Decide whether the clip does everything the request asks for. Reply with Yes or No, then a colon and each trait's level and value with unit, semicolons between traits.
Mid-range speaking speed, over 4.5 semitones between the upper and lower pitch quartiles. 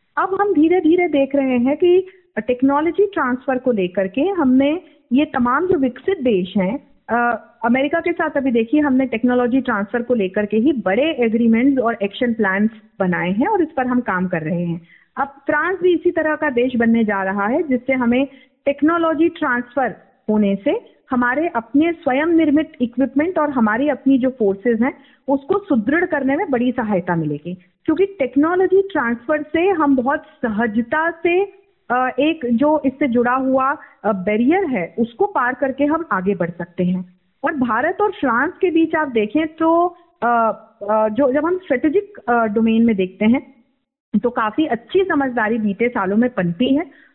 Yes: average, 165 wpm; average, 5.1 semitones